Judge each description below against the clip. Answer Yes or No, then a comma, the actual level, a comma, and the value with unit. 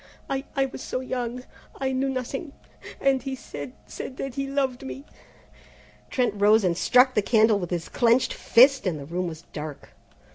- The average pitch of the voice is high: Yes, very high, 250 Hz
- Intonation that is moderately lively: No, wide, 6.5 semitones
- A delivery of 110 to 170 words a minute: No, average, 185 wpm